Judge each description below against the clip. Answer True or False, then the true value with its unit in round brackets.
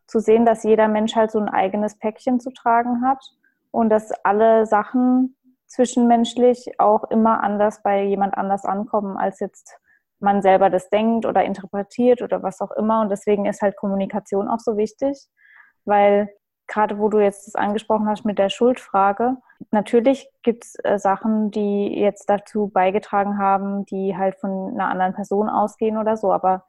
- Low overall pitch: False (210 Hz)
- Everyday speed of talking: True (170 wpm)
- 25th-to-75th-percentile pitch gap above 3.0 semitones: False (2.7 semitones)